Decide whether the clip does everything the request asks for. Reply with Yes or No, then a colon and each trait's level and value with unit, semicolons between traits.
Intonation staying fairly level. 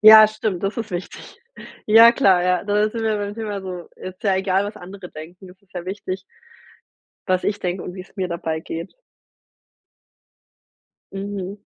Yes: narrow, 2.3 semitones